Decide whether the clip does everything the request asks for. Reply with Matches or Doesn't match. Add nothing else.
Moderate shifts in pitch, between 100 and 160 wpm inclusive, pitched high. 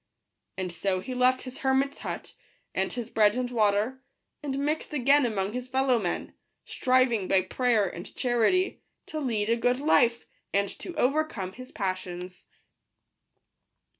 Matches